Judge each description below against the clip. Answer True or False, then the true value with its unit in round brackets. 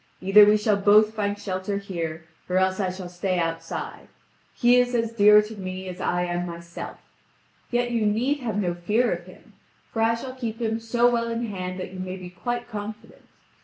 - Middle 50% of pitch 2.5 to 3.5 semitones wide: False (3.9 semitones)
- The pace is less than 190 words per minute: False (200 wpm)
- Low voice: False (205 Hz)